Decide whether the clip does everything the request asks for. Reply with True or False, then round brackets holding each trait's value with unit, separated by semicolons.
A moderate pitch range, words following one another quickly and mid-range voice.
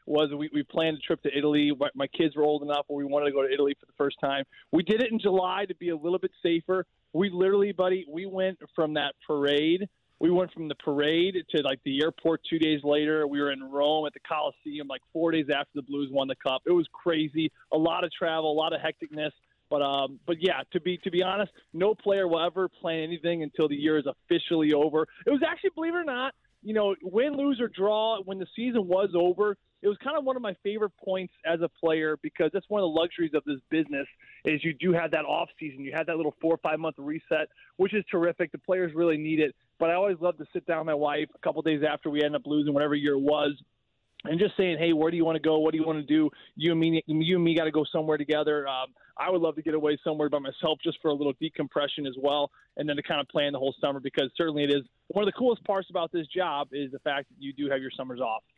True (3.5 semitones; 270 wpm; 160 Hz)